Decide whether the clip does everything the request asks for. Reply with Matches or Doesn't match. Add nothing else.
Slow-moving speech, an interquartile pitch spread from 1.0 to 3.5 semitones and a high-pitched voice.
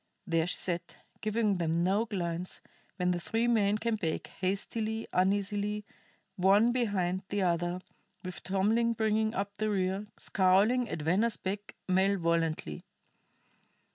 Matches